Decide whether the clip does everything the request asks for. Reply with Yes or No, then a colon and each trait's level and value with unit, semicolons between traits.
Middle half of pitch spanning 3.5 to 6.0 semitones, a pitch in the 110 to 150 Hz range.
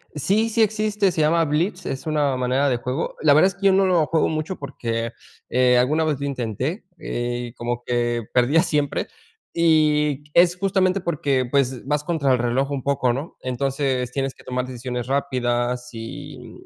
Yes: average, 4.5 semitones; medium, 140 Hz